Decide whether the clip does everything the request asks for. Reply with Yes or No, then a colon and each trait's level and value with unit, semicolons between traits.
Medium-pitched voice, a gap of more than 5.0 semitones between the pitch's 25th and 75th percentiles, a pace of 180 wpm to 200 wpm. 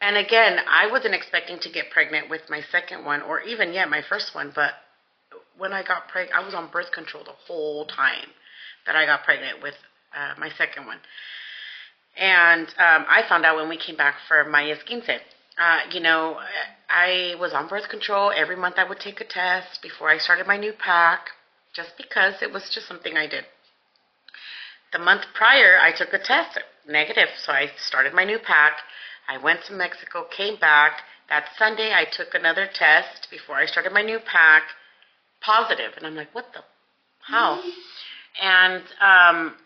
No: medium, 180 Hz; average, 4.1 semitones; average, 185 wpm